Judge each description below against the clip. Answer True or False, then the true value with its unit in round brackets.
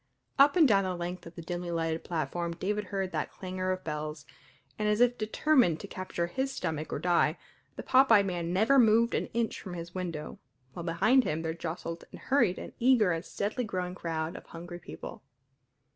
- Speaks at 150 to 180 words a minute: False (200 wpm)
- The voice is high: False (180 Hz)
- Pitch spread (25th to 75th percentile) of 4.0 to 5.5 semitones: True (4.3 semitones)